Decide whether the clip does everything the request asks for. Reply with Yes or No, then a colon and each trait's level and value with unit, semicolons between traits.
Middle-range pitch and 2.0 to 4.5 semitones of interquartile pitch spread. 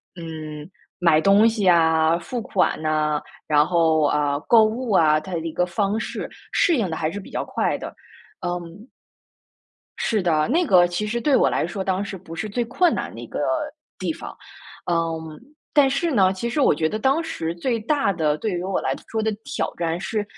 No: medium, 180 Hz; average, 5.3 semitones